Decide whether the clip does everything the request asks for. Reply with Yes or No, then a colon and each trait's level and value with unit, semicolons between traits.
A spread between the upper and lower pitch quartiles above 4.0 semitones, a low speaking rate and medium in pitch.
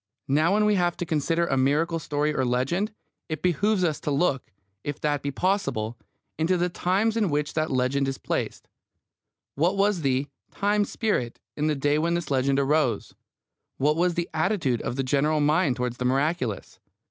No: average, 4.4 semitones; average, 185 wpm; medium, 155 Hz